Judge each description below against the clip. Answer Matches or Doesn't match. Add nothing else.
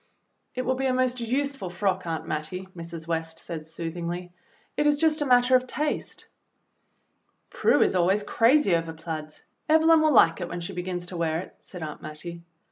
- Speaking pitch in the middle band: Matches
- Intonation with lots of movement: Matches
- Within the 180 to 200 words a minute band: Matches